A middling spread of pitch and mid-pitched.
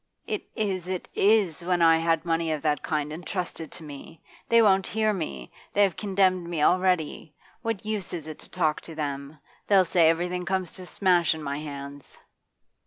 Yes: average, 3.3 semitones; medium, 170 Hz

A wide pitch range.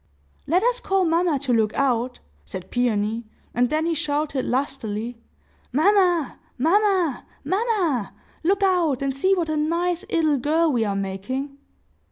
Yes: wide, 6.2 semitones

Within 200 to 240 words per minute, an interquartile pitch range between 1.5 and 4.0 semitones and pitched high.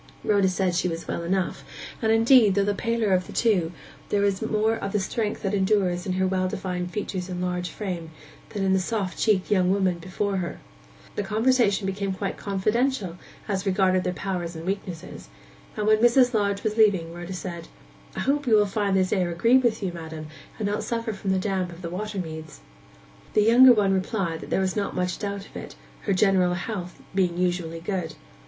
Yes: fast, 205 wpm; average, 2.7 semitones; high, 195 Hz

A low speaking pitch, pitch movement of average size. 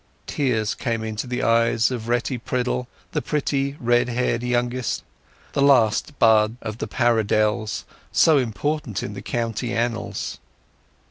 No: low, 120 Hz; narrow, 2.1 semitones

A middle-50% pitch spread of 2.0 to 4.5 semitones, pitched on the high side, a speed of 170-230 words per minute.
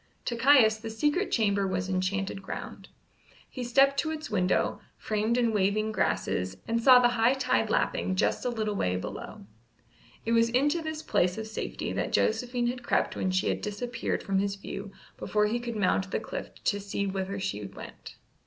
Yes: average, 3.9 semitones; high, 220 Hz; average, 185 wpm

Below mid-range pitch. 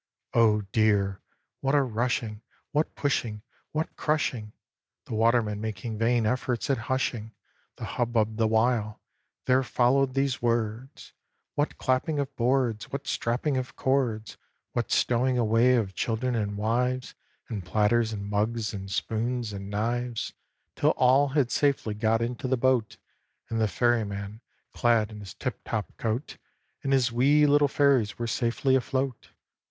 Yes: low, 120 Hz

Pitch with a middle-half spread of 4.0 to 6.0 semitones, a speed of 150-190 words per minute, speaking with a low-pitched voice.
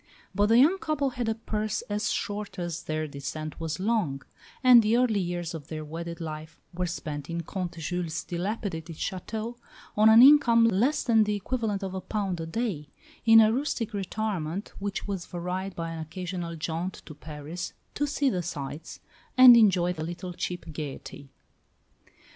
No: average, 5.1 semitones; average, 170 wpm; medium, 185 Hz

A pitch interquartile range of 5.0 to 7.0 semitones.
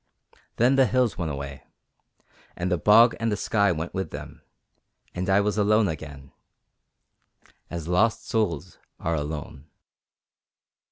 Yes: average, 5.3 semitones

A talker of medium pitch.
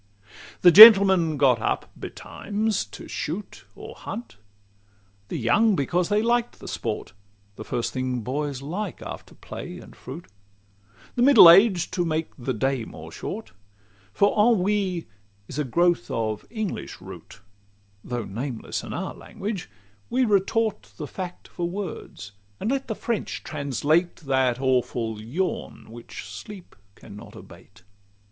Yes: medium, 170 Hz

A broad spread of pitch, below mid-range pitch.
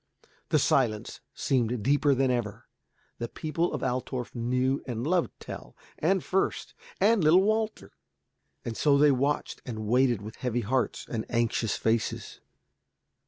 No: average, 4.1 semitones; low, 130 Hz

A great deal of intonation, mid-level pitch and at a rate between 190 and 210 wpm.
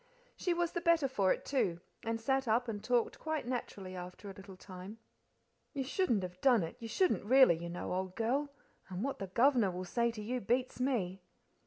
No: wide, 6.0 semitones; high, 230 Hz; fast, 205 wpm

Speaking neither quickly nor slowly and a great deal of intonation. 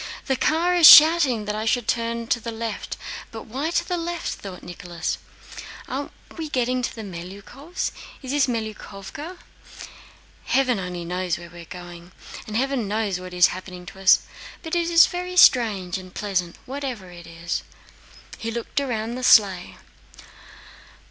Yes: average, 160 wpm; wide, 6.8 semitones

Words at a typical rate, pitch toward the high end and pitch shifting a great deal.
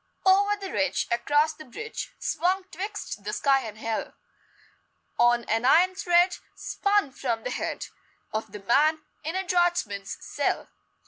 Yes: average, 145 wpm; very high, 310 Hz; wide, 7.6 semitones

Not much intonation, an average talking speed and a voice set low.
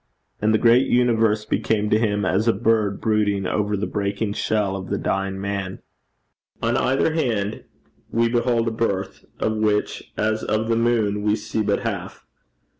Yes: narrow, 2.0 semitones; average, 170 wpm; low, 110 Hz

